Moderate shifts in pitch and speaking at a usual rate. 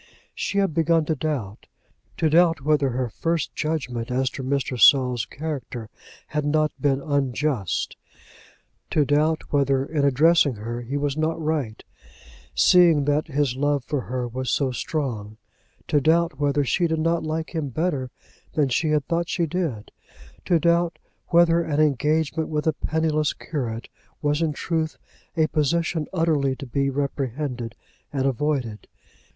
Yes: average, 3.3 semitones; average, 150 wpm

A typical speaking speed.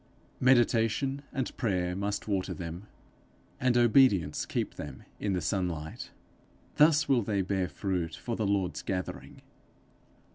No: slow, 130 wpm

